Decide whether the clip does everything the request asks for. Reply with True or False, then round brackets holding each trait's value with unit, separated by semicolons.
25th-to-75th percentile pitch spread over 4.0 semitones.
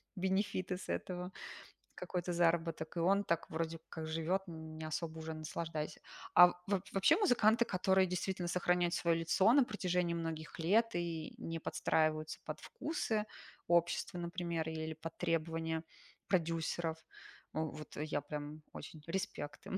False (2.5 semitones)